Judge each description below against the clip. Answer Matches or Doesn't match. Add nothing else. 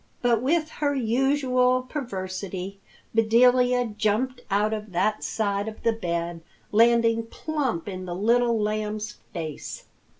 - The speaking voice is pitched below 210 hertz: Doesn't match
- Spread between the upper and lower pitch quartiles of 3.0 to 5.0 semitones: Matches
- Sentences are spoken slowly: Matches